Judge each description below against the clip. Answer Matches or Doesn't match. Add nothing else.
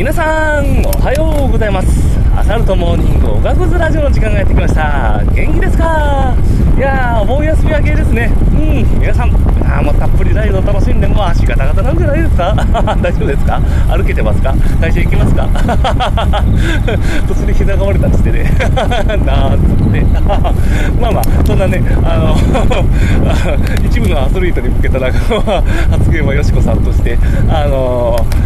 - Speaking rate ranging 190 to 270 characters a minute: Doesn't match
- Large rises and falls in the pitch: Doesn't match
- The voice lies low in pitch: Matches